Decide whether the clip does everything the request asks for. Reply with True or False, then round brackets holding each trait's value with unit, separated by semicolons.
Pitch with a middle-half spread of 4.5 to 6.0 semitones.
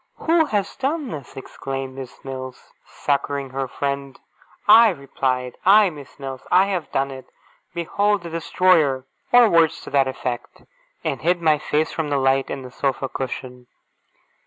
True (5.2 semitones)